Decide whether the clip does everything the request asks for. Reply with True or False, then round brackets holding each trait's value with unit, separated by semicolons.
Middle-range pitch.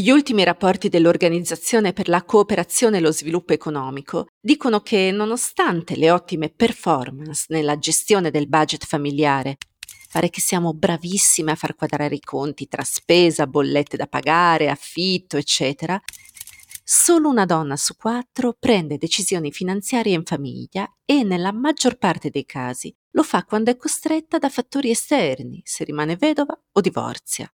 True (175 Hz)